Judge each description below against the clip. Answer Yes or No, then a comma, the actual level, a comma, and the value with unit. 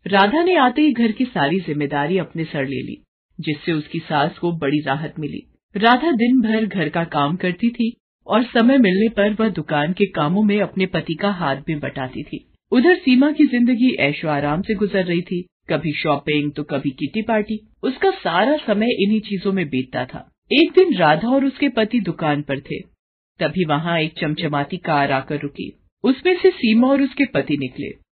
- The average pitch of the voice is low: No, medium, 185 Hz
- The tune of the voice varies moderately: No, wide, 7.8 semitones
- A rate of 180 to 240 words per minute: Yes, fast, 190 wpm